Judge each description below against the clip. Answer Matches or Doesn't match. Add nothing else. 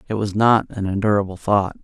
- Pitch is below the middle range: Matches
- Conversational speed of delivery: Matches